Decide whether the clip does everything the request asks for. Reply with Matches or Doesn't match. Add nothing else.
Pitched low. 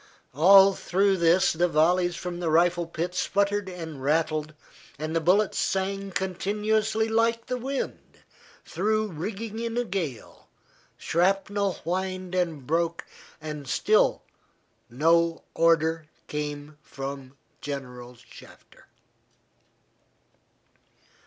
Doesn't match